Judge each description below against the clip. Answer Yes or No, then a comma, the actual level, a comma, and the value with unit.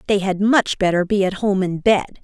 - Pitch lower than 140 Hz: No, high, 195 Hz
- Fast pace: Yes, fast, 240 wpm